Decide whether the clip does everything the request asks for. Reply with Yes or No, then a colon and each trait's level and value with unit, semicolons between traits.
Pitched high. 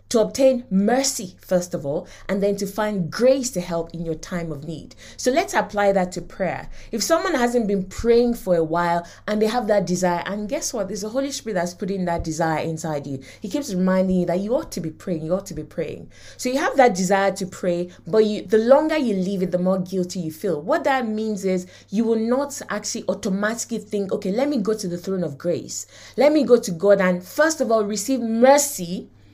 Yes: high, 200 Hz